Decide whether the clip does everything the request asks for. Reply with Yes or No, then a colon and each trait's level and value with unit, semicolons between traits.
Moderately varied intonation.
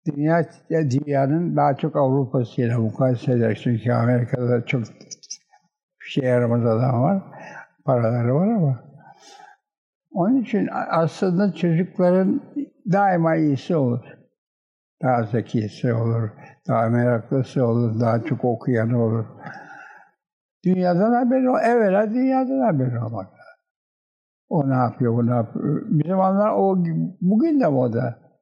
No: wide, 8.2 semitones